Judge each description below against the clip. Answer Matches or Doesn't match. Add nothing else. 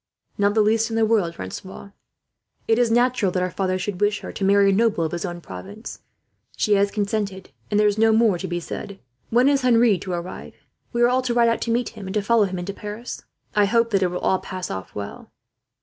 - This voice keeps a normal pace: Doesn't match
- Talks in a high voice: Matches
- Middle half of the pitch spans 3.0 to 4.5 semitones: Matches